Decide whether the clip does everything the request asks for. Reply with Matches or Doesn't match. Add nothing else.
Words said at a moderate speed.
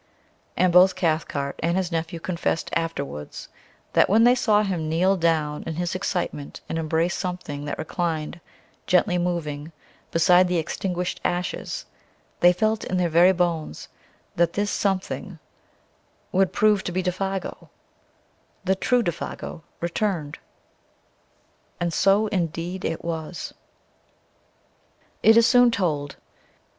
Doesn't match